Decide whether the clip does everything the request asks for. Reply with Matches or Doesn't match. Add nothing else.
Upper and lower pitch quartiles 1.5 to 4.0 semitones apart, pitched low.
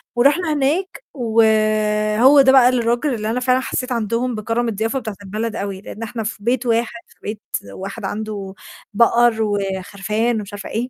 Doesn't match